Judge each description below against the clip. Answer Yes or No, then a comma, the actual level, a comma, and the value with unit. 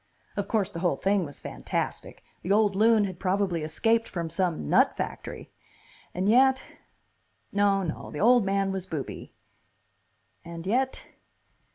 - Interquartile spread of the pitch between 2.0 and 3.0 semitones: No, average, 3.6 semitones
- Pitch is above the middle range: Yes, high, 195 Hz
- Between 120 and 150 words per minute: Yes, average, 145 wpm